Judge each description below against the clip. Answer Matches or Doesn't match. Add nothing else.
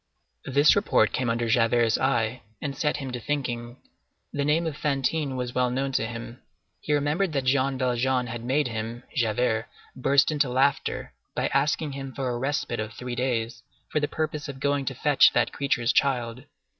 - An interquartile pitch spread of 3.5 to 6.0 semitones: Doesn't match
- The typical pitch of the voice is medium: Doesn't match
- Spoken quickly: Doesn't match